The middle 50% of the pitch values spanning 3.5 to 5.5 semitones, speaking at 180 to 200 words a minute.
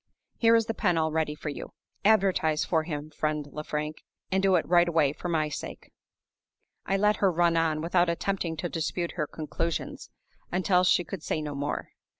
No: average, 3.0 semitones; average, 185 wpm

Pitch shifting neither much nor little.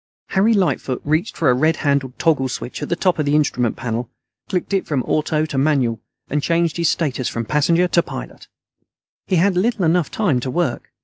Yes: average, 4.8 semitones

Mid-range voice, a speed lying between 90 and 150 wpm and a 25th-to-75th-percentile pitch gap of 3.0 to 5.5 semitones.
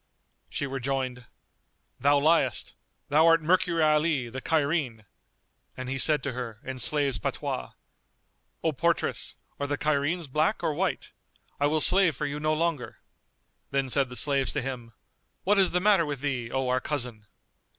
No: medium, 145 Hz; average, 160 wpm; average, 3.6 semitones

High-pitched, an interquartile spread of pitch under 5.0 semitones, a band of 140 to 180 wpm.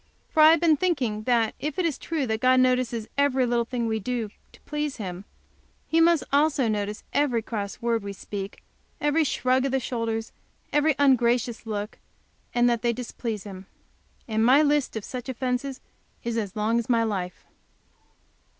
Yes: high, 240 Hz; average, 3.9 semitones; average, 175 wpm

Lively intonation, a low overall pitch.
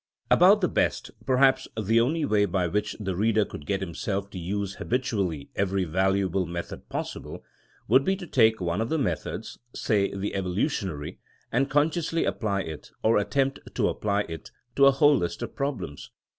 Yes: wide, 5.7 semitones; low, 105 Hz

